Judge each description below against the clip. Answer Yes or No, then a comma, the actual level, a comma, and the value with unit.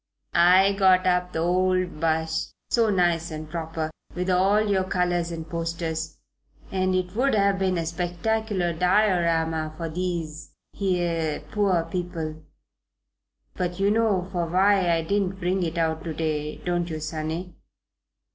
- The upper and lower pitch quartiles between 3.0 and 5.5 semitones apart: No, narrow, 2.4 semitones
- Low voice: No, medium, 175 Hz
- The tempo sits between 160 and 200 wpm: No, average, 145 wpm